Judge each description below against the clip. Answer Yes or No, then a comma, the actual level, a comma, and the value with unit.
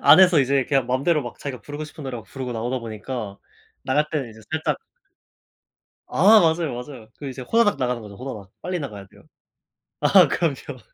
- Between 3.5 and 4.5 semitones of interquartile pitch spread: Yes, average, 4.1 semitones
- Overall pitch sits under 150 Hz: Yes, low, 135 Hz